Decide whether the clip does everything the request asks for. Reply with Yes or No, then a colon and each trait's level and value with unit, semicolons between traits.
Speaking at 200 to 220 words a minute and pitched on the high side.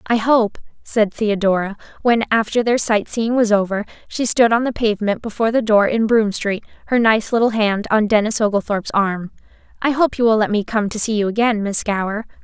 Yes: fast, 205 wpm; high, 215 Hz